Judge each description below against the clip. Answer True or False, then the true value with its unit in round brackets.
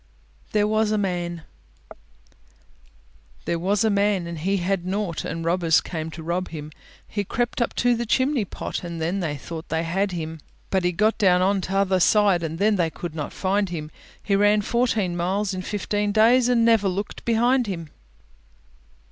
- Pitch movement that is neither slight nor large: True (3.6 semitones)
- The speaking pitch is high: True (195 Hz)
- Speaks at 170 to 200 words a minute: True (180 wpm)